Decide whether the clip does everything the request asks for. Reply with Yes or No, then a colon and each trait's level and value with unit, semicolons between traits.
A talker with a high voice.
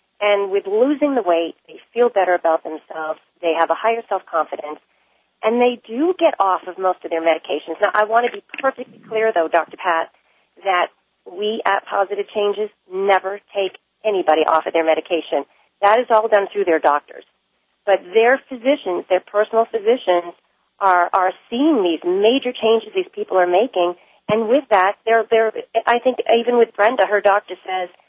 Yes: high, 205 Hz